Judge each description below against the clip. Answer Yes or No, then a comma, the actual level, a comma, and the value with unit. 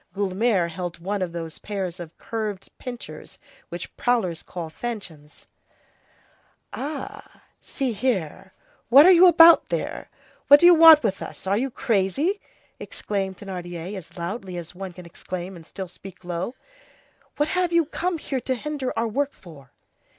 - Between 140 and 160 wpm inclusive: Yes, average, 155 wpm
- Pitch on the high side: Yes, high, 200 Hz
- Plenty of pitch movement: Yes, wide, 7.2 semitones